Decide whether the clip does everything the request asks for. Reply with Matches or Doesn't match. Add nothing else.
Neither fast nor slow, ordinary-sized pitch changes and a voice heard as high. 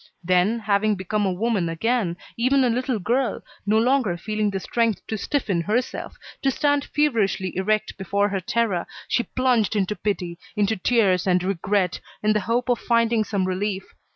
Matches